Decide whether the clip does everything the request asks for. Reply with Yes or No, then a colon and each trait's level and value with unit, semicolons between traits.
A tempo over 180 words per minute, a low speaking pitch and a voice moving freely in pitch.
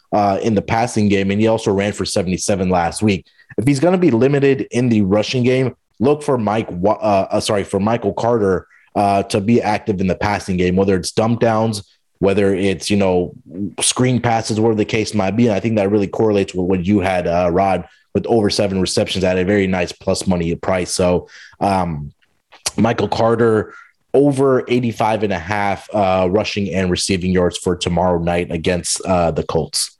No: average, 200 wpm; low, 100 Hz; average, 3.3 semitones